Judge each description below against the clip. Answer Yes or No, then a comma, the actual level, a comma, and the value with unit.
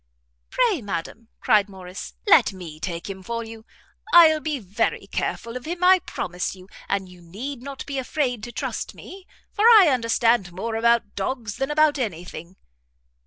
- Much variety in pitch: Yes, wide, 7.0 semitones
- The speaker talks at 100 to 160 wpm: No, average, 170 wpm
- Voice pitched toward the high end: Yes, high, 230 Hz